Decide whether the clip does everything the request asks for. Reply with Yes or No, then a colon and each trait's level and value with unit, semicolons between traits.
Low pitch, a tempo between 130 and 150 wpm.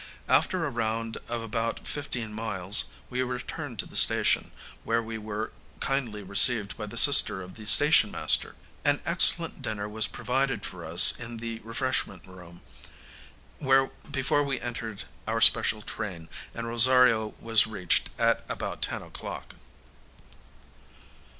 Yes: low, 115 Hz; slow, 135 wpm